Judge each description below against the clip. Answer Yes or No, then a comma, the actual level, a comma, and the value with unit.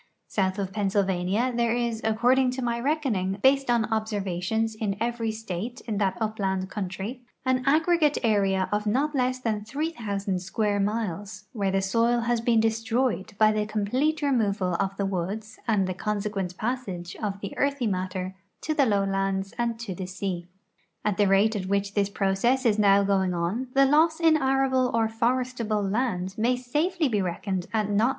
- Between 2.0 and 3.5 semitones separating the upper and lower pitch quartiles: No, average, 3.9 semitones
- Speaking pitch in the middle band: No, high, 215 Hz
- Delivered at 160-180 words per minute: Yes, average, 175 wpm